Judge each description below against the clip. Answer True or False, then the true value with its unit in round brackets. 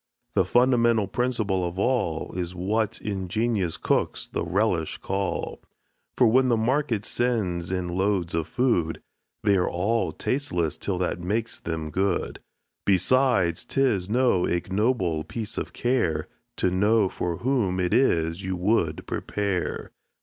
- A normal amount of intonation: True (4.8 semitones)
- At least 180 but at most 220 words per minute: False (135 wpm)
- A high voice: False (100 Hz)